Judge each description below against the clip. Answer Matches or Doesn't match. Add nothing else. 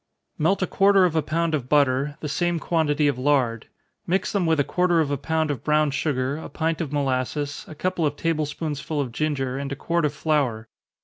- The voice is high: Doesn't match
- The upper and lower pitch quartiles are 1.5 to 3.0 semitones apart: Matches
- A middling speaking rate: Doesn't match